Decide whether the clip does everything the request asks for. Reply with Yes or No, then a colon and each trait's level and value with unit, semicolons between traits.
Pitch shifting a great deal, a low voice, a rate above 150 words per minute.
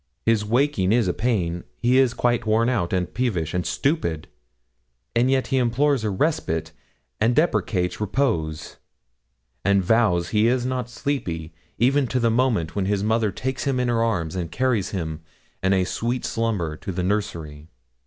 Yes: wide, 5.8 semitones; low, 110 Hz; average, 170 wpm